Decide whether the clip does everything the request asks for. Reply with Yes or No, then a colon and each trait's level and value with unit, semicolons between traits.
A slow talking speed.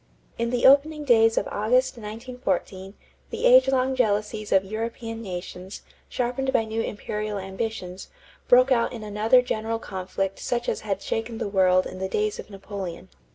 No: average, 165 wpm